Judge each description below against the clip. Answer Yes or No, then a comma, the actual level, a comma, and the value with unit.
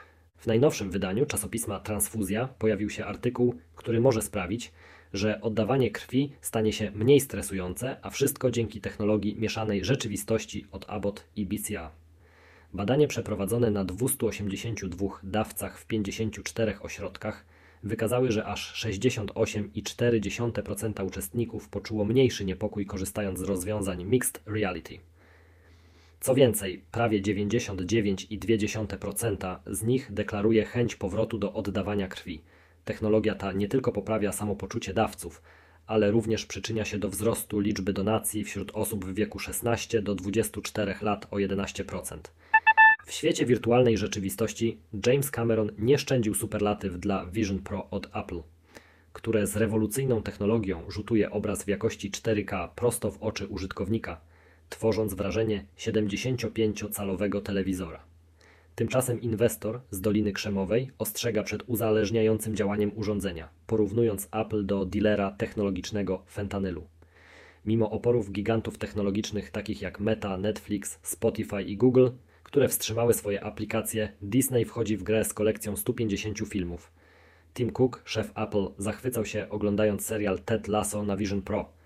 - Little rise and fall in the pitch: Yes, narrow, 2.2 semitones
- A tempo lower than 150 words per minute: Yes, average, 125 wpm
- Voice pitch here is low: Yes, low, 105 Hz